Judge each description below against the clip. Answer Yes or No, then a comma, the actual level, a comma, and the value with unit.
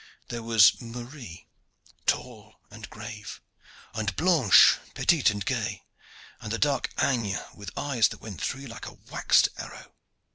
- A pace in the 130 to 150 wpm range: Yes, average, 145 wpm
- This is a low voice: Yes, low, 115 Hz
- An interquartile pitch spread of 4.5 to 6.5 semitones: No, average, 3.4 semitones